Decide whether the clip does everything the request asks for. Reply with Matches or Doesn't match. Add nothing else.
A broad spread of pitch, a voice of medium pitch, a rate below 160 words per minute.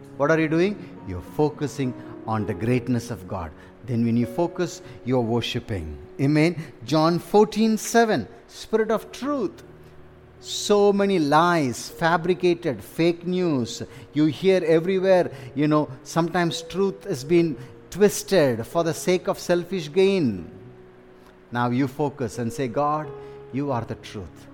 Matches